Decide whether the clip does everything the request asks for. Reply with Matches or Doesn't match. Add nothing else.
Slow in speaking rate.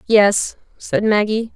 Matches